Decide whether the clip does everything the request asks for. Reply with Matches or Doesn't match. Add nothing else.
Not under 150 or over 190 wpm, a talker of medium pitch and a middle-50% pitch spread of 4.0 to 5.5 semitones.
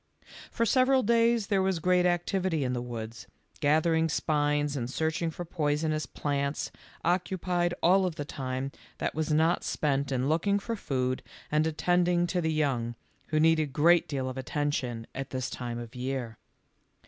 Matches